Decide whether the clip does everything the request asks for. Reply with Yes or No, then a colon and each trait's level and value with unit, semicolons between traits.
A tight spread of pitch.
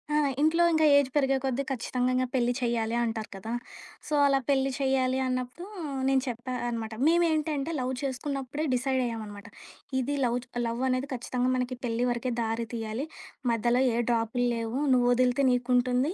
Yes: narrow, 2.2 semitones